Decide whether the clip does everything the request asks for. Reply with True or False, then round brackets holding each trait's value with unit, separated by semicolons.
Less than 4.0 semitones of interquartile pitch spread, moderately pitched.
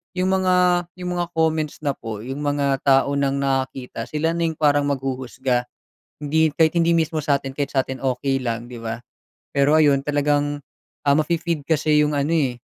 True (3.1 semitones; 145 Hz)